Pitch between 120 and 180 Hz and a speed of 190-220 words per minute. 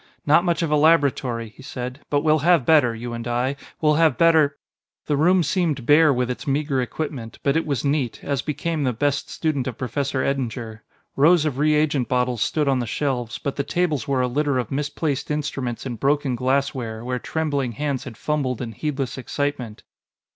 Yes: medium, 140 Hz; average, 195 wpm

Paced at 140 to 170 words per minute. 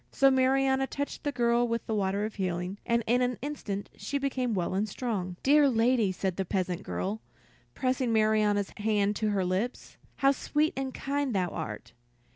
No: average, 180 wpm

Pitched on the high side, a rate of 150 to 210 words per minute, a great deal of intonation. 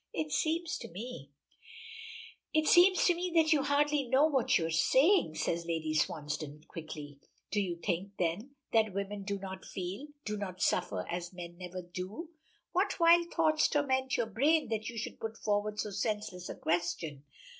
Yes: high, 210 Hz; average, 175 wpm; wide, 9.0 semitones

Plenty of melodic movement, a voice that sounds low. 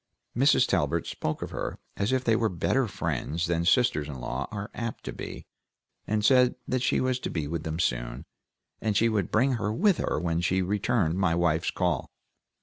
Yes: wide, 6.0 semitones; very low, 95 Hz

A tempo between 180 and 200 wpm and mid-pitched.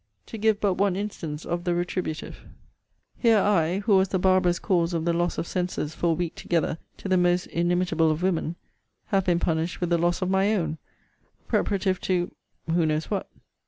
Yes: average, 195 wpm; medium, 175 Hz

